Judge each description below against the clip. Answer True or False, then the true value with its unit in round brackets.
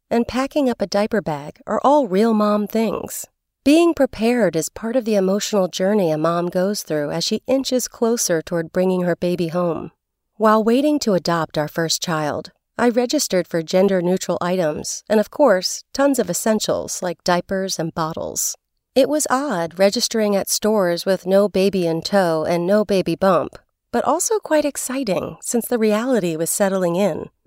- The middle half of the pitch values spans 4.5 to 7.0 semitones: True (5.1 semitones)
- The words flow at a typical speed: True (175 wpm)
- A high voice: True (200 Hz)